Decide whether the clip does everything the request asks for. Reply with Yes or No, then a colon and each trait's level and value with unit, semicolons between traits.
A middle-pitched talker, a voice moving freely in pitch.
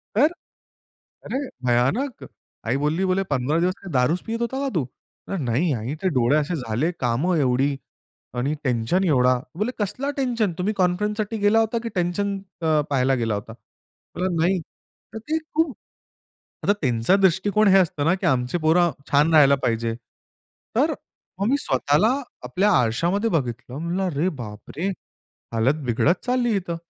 Yes: medium, 170 Hz; wide, 7.7 semitones